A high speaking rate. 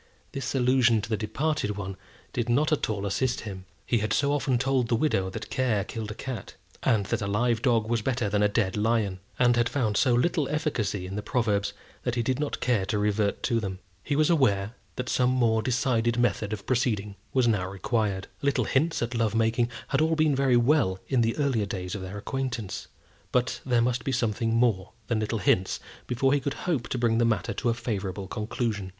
Yes: fast, 215 wpm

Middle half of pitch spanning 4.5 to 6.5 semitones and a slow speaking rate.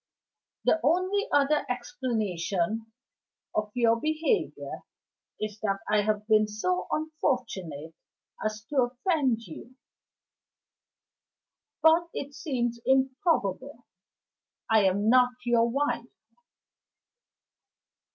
Yes: average, 5.1 semitones; slow, 90 wpm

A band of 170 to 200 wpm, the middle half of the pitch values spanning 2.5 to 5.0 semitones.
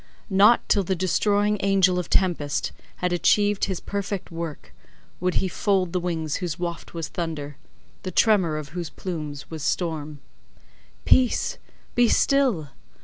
No: average, 140 wpm; average, 3.6 semitones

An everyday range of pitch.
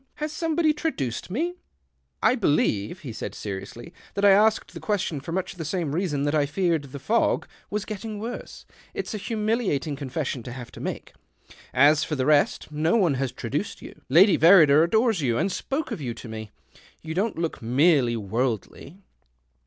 No: wide, 7.7 semitones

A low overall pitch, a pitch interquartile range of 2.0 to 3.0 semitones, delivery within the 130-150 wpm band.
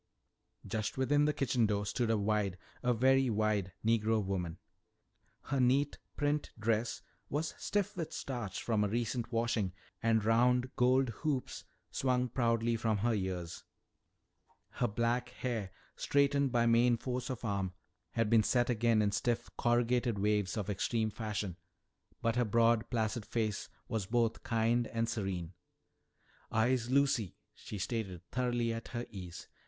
Yes: low, 115 Hz; average, 2.7 semitones; average, 145 wpm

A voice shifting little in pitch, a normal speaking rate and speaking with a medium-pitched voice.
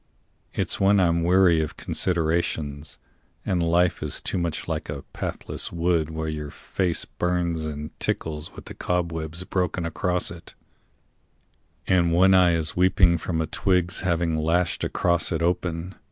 No: narrow, 2.0 semitones; average, 150 wpm; very low, 85 Hz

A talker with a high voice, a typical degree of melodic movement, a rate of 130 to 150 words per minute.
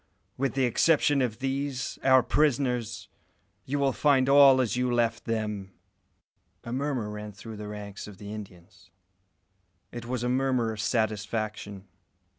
No: low, 120 Hz; average, 3.9 semitones; average, 145 wpm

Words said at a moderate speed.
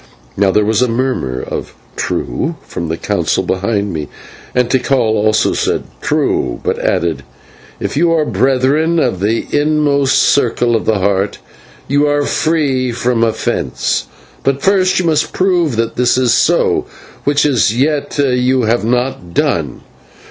Yes: average, 150 wpm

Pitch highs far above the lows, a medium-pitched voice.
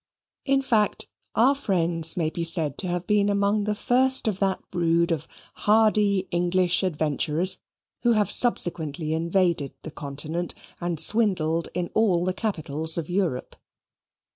No: average, 4.1 semitones; medium, 180 Hz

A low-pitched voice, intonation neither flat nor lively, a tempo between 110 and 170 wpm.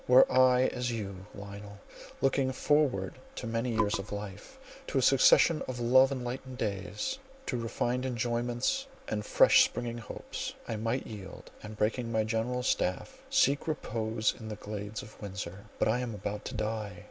Yes: low, 115 Hz; average, 3.3 semitones; average, 165 wpm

